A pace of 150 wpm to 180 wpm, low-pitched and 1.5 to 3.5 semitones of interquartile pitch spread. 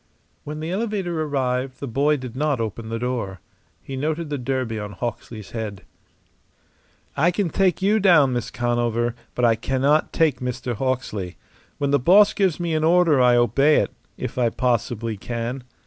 No: average, 170 wpm; low, 130 Hz; average, 4.6 semitones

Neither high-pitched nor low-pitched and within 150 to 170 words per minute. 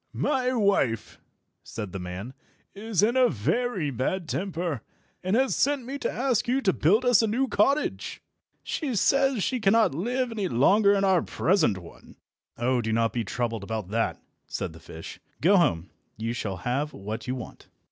No: medium, 180 Hz; average, 180 wpm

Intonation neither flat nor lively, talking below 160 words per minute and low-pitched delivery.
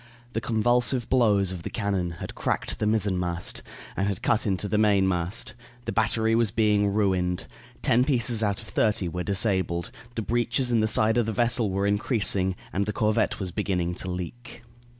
No: average, 3.3 semitones; average, 180 wpm; low, 105 Hz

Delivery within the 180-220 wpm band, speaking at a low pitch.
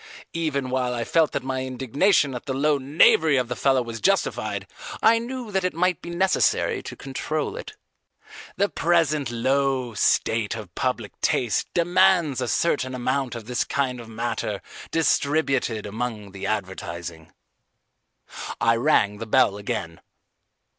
No: average, 145 wpm; low, 130 Hz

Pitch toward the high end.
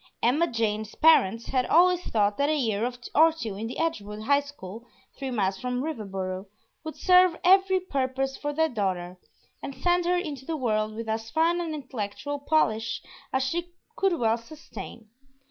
Yes: very high, 265 Hz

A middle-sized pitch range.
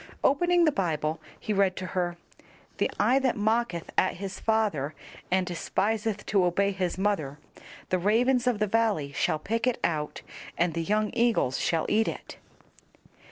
Yes: average, 4.5 semitones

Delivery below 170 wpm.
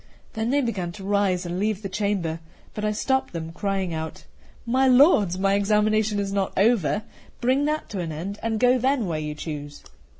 No: average, 195 wpm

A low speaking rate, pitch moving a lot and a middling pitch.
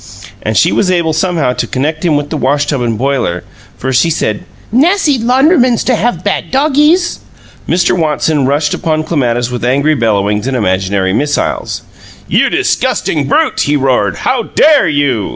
No: average, 165 wpm; wide, 7.3 semitones; medium, 150 Hz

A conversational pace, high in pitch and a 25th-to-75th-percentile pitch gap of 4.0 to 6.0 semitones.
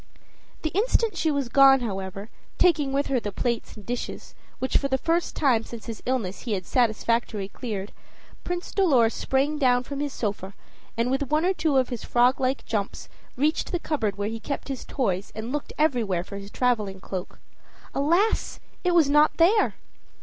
Yes: average, 185 wpm; very high, 255 Hz; average, 5.3 semitones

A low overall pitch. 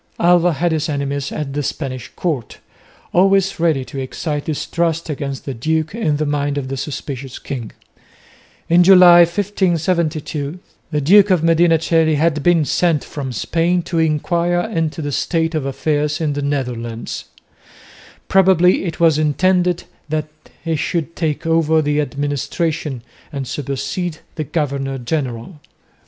No: medium, 155 Hz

